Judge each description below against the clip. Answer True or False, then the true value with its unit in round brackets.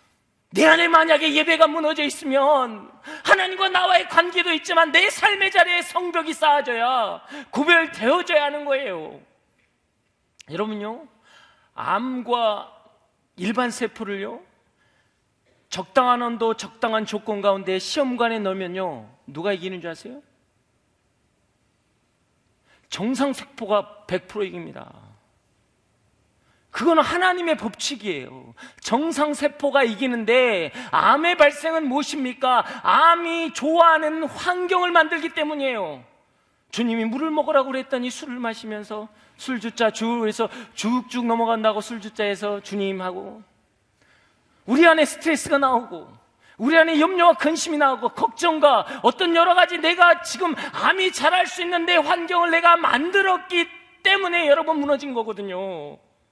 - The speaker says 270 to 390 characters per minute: True (275 characters per minute)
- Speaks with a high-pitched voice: True (275 Hz)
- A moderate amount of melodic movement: False (7.2 semitones)